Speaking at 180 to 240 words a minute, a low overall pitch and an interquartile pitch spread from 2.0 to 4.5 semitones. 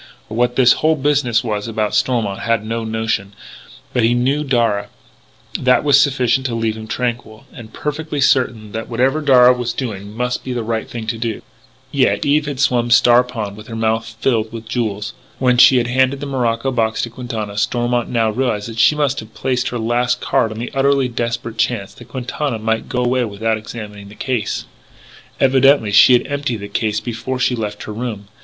Yes: average, 195 wpm; low, 120 Hz; narrow, 2.5 semitones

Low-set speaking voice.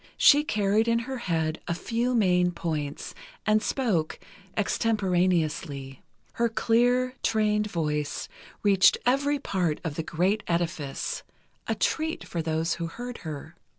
No: high, 190 Hz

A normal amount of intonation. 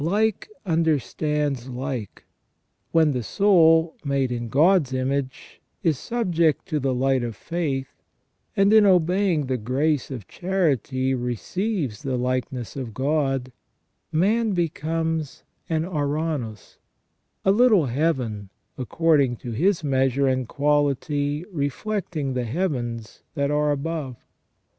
Yes: average, 4.3 semitones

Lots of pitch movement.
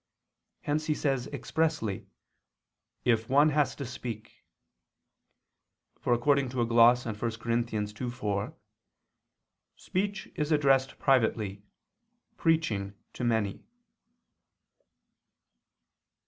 No: average, 4.5 semitones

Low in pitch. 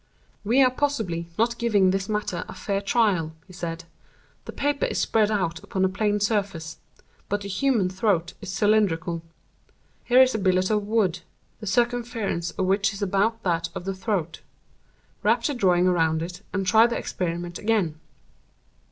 No: high, 195 Hz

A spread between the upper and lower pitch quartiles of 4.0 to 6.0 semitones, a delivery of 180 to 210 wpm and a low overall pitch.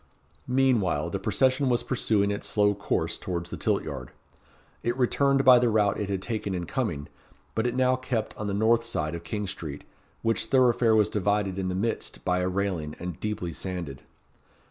Yes: average, 4.7 semitones; average, 190 wpm; low, 105 Hz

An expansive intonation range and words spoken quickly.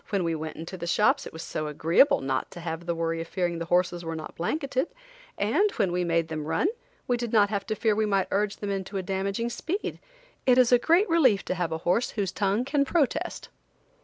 Yes: wide, 6.1 semitones; fast, 235 wpm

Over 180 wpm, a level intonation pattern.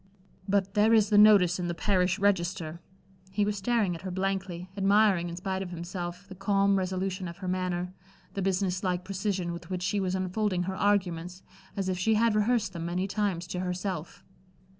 Yes: average, 190 wpm; narrow, 2.0 semitones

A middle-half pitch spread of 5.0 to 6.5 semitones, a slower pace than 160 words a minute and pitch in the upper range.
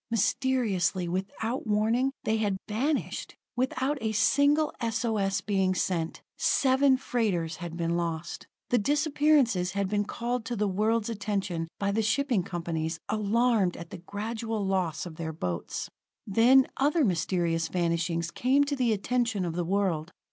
Yes: wide, 5.6 semitones; average, 150 wpm; high, 205 Hz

